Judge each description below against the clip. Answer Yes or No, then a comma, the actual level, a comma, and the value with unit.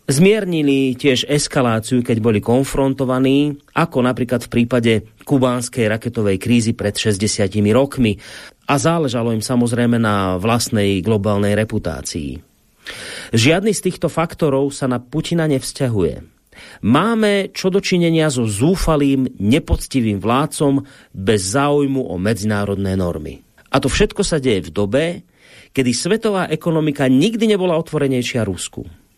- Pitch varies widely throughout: Yes, wide, 5.8 semitones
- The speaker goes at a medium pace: Yes, average, 120 wpm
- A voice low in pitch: Yes, low, 130 Hz